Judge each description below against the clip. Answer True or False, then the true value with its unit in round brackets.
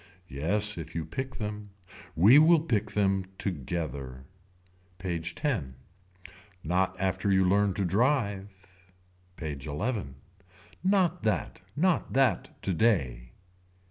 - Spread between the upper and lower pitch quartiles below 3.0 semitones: False (4.8 semitones)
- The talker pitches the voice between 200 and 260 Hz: False (95 Hz)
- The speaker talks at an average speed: False (110 wpm)